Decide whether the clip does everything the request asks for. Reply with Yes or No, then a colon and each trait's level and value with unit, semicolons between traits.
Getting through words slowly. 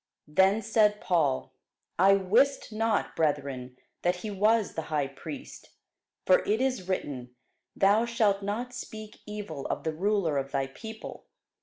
No: average, 145 wpm